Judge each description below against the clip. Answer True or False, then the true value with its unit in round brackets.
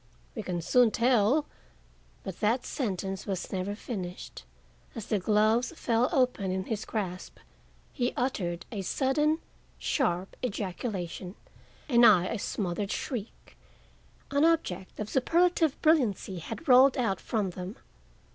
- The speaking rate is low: True (130 wpm)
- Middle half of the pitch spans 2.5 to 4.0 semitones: False (5.1 semitones)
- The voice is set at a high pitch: True (215 Hz)